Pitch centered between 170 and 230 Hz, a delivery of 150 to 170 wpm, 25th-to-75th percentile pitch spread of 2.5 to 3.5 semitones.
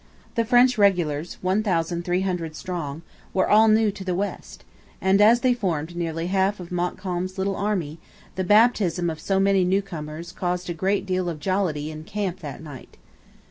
Yes: medium, 185 Hz; average, 165 wpm; average, 2.9 semitones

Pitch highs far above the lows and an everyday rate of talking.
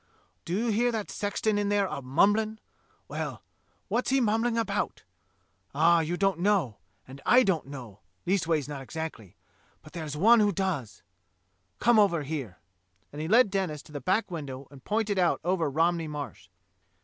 Yes: wide, 5.8 semitones; average, 165 wpm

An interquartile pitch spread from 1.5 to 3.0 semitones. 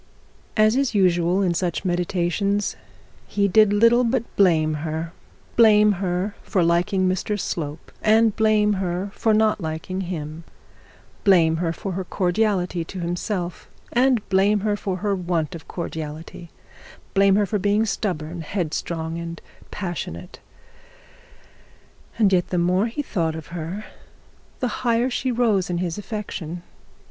No: average, 3.6 semitones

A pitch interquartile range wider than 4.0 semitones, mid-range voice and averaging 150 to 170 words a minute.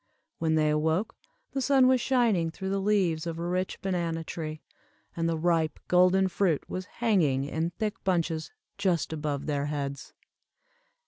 No: average, 3.4 semitones; medium, 170 Hz; average, 155 wpm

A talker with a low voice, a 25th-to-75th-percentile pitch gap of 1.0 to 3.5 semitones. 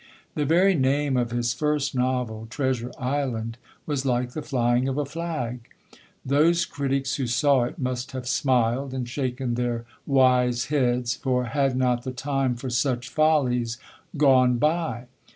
Yes: low, 130 Hz; narrow, 2.5 semitones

